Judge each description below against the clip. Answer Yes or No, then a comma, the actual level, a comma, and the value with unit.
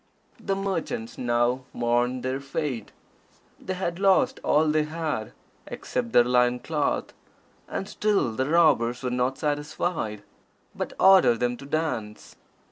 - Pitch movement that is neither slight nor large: Yes, average, 4.9 semitones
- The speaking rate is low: Yes, slow, 130 wpm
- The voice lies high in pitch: No, low, 135 Hz